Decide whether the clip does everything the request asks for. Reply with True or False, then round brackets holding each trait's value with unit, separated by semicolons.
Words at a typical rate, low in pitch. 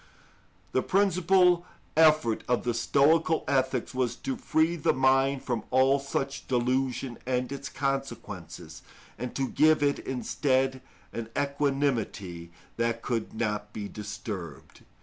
False (125 wpm; 130 Hz)